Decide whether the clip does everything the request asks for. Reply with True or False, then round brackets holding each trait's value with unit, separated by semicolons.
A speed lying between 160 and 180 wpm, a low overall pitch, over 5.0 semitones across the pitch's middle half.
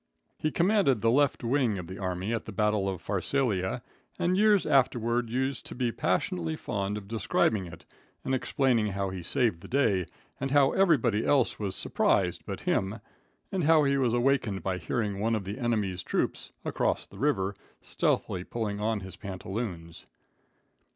True (170 wpm; 110 Hz; 5.4 semitones)